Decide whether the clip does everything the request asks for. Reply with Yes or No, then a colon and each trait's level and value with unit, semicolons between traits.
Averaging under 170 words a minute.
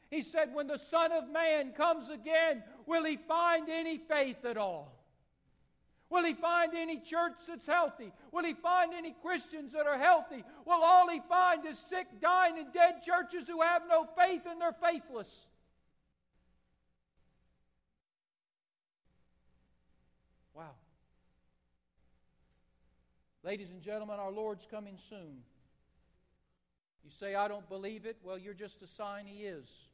Yes: average, 140 wpm